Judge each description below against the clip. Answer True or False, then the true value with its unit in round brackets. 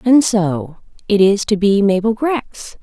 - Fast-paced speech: False (170 wpm)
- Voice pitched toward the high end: True (210 Hz)